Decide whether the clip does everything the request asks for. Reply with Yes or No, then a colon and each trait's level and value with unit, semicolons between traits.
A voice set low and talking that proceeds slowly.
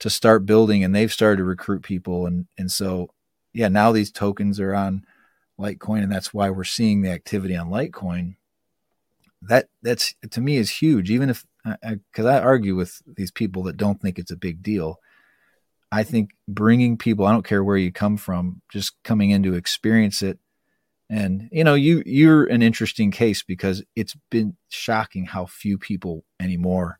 No: low, 100 Hz; average, 180 wpm